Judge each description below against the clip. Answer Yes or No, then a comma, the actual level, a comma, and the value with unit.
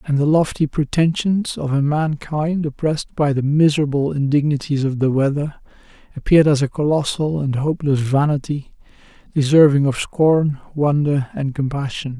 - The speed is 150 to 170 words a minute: No, average, 140 wpm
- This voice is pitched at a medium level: Yes, medium, 145 Hz